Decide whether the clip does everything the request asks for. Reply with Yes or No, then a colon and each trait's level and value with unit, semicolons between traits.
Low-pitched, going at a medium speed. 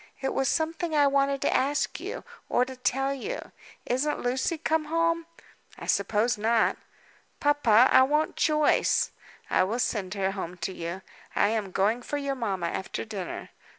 No: very high, 260 Hz; average, 165 wpm